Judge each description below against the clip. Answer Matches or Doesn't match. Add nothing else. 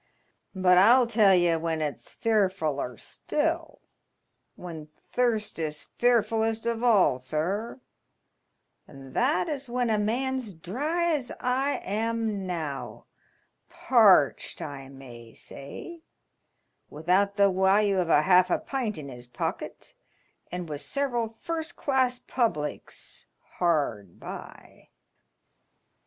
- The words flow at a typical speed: Doesn't match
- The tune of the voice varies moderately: Doesn't match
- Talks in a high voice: Matches